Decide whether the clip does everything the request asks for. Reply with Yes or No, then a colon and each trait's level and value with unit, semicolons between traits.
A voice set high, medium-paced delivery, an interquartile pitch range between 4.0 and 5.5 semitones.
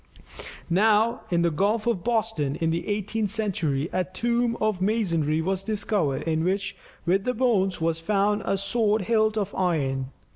Yes: high, 195 Hz; average, 160 wpm; average, 4.5 semitones